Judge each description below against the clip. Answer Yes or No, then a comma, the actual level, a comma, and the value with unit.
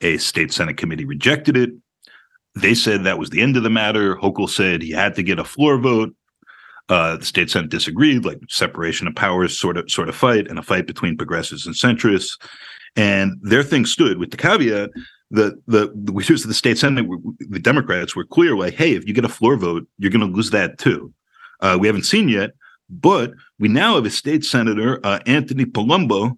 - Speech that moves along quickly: Yes, fast, 215 wpm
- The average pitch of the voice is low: Yes, low, 110 Hz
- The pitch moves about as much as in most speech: Yes, average, 3.7 semitones